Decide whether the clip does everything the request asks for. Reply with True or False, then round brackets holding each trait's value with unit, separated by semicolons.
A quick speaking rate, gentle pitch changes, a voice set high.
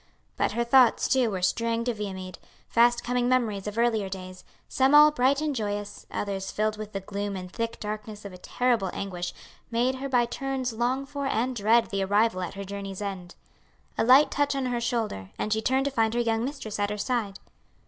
False (210 wpm; 3.8 semitones; 225 Hz)